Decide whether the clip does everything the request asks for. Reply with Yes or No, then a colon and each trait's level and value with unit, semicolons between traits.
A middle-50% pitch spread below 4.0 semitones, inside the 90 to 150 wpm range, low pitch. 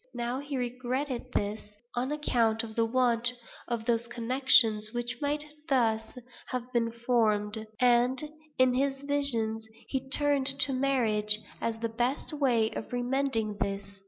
No: average, 2.9 semitones; average, 140 wpm; high, 240 Hz